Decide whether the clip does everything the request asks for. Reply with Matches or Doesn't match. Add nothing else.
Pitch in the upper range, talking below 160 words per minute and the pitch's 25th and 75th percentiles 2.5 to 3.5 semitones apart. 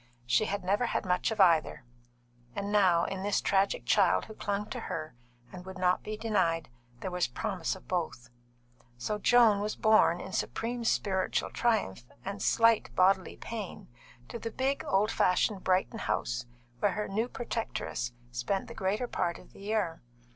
Doesn't match